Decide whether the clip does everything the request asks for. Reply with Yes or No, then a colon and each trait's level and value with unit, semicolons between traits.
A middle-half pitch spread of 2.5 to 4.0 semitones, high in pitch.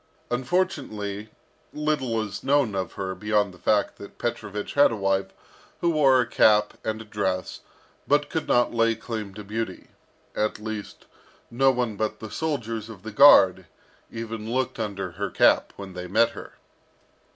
No: average, 3.3 semitones; low, 110 Hz